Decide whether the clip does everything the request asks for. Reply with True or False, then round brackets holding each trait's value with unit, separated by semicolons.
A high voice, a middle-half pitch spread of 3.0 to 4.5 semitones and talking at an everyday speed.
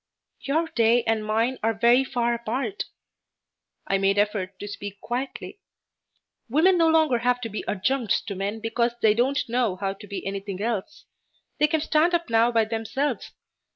True (230 Hz; 4.2 semitones; 170 wpm)